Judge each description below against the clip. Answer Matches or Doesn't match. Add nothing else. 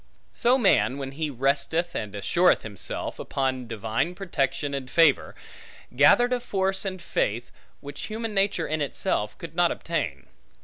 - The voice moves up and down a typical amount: Doesn't match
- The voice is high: Doesn't match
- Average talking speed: Matches